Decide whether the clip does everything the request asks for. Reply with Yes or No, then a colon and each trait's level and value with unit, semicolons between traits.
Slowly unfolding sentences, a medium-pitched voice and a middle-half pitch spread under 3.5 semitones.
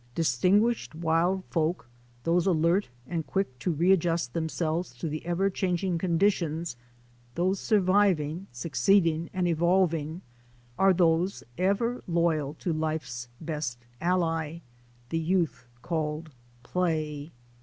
Yes: slow, 120 wpm; medium, 165 Hz; average, 2.8 semitones